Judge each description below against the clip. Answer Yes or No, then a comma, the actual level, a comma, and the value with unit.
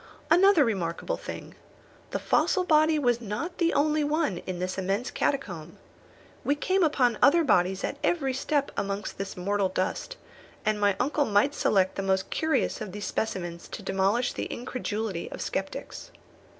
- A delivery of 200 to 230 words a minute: No, average, 160 wpm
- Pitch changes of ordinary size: No, wide, 7.6 semitones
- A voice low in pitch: No, high, 225 Hz